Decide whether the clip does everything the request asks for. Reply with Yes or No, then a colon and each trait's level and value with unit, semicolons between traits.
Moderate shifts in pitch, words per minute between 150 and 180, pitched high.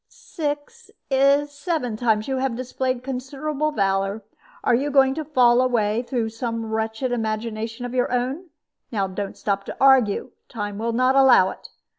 Yes: average, 3.6 semitones; average, 165 wpm; high, 245 Hz